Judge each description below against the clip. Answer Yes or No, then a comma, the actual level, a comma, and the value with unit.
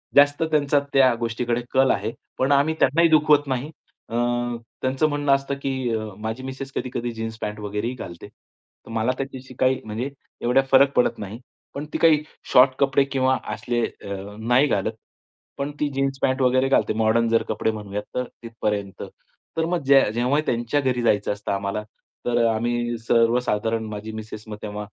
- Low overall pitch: Yes, low, 125 Hz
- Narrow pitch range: No, average, 3.7 semitones